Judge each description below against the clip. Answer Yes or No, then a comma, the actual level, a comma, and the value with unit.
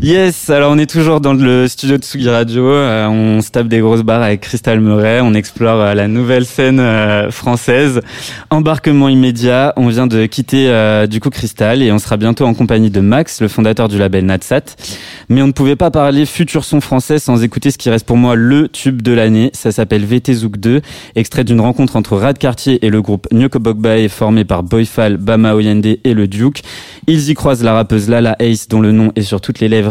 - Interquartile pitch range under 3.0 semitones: No, average, 3.4 semitones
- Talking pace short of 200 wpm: No, fast, 220 wpm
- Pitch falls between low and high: No, low, 120 Hz